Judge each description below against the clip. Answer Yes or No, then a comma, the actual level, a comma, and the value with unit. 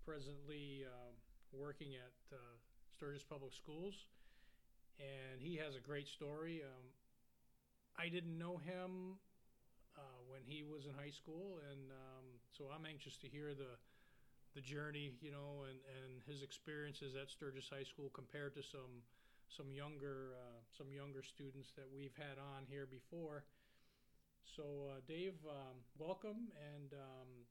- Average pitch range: No, narrow, 2.2 semitones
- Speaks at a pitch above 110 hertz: Yes, medium, 140 Hz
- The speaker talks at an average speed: Yes, average, 150 wpm